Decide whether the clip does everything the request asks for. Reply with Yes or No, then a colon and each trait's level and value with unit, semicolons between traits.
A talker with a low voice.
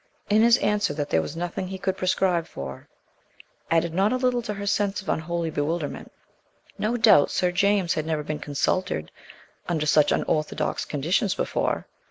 No: medium, 175 Hz